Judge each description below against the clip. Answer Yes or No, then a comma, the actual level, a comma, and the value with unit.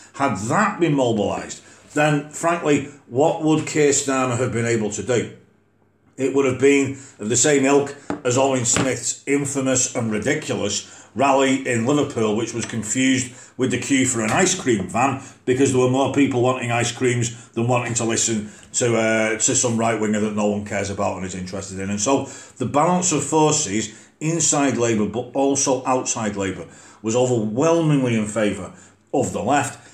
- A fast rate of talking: No, average, 180 wpm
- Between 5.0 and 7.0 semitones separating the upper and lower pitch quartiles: No, average, 4.0 semitones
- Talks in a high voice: No, low, 125 Hz